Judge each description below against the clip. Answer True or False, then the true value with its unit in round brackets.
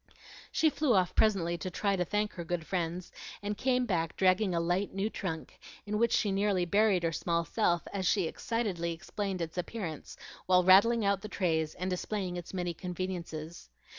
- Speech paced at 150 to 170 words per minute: False (185 wpm)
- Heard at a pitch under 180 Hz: False (185 Hz)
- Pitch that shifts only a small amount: False (3.1 semitones)